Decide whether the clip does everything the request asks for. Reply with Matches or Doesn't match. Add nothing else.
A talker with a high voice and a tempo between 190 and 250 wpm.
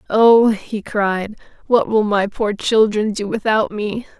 Doesn't match